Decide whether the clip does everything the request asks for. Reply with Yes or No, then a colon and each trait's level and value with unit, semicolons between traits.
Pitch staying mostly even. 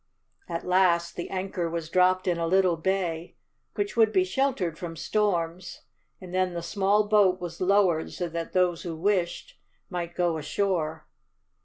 Yes: narrow, 2.2 semitones